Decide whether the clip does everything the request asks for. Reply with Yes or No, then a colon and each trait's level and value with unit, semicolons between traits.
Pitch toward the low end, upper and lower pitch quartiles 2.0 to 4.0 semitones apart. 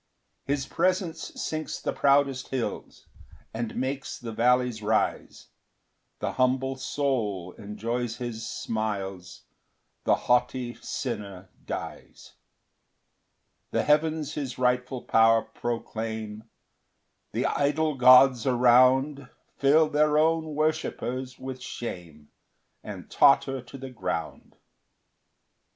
Yes: low, 125 Hz; average, 3.6 semitones